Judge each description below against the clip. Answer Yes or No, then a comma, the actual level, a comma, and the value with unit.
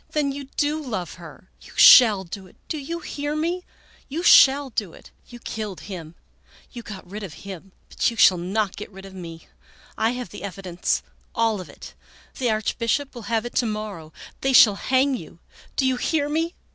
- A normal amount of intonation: No, wide, 6.0 semitones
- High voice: Yes, high, 220 Hz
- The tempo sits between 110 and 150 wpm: No, average, 200 wpm